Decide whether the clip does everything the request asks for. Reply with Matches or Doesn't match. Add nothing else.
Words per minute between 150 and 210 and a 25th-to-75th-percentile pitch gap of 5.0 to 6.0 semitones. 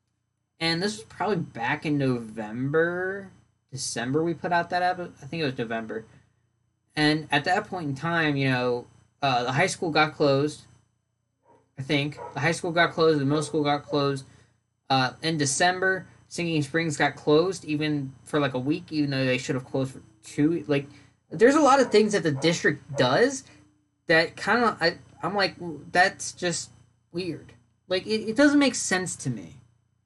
Matches